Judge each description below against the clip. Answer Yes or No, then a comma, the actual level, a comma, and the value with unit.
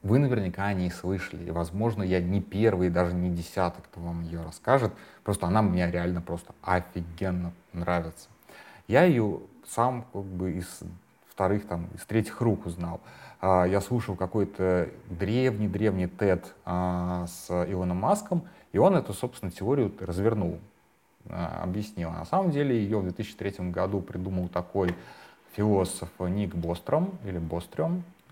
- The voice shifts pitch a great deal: No, average, 3.5 semitones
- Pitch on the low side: Yes, very low, 95 Hz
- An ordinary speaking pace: Yes, average, 140 wpm